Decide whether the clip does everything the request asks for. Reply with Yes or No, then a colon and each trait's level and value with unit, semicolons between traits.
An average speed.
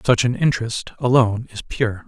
Yes: average, 175 wpm